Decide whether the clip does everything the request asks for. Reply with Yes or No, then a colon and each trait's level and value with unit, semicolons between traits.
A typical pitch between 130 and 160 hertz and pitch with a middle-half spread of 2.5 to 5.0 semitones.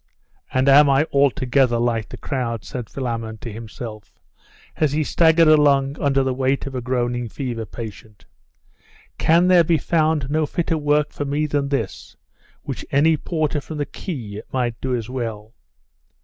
Yes: low, 135 Hz; average, 4.0 semitones